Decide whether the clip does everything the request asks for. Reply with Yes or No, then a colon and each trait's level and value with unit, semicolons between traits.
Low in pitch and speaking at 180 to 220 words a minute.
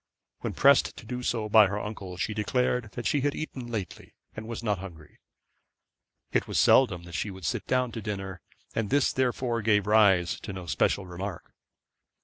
Yes: low, 105 Hz; average, 185 wpm